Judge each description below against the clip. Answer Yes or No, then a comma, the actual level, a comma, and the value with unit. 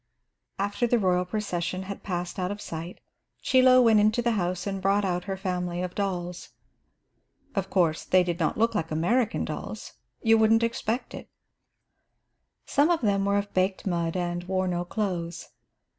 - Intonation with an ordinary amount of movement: Yes, average, 3.3 semitones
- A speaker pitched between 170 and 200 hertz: Yes, high, 190 Hz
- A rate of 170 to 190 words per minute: Yes, average, 175 wpm